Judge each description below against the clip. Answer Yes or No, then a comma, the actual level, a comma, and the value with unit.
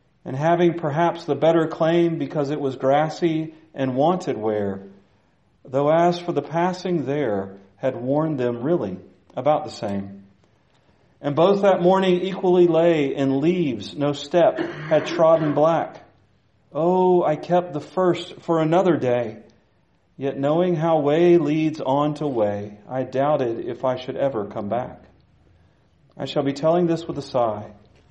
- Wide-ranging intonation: No, average, 4.6 semitones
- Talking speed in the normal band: Yes, average, 150 wpm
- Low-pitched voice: No, medium, 150 Hz